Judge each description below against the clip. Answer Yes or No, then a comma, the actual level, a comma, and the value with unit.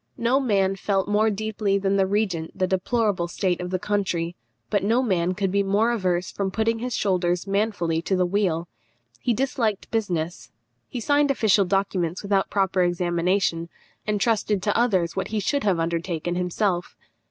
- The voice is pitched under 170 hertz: No, high, 195 Hz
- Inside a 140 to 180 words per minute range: Yes, average, 170 wpm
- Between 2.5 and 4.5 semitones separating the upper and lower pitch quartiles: Yes, average, 3.1 semitones